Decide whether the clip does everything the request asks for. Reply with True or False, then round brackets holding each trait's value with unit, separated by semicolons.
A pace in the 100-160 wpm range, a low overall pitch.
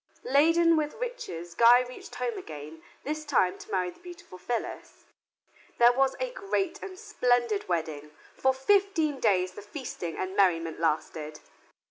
False (145 wpm; 245 Hz)